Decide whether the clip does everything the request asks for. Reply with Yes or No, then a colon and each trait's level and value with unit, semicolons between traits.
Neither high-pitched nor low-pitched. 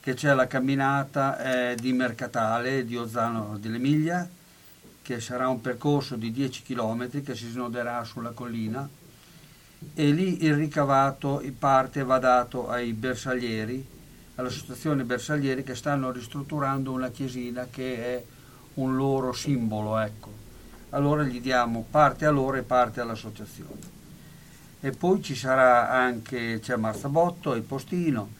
No: low, 130 Hz